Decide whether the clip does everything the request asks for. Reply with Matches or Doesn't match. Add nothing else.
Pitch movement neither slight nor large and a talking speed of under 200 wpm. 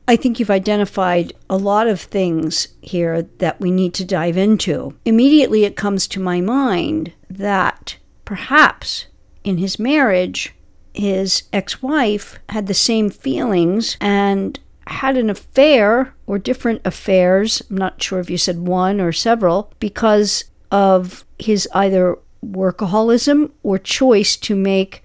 Matches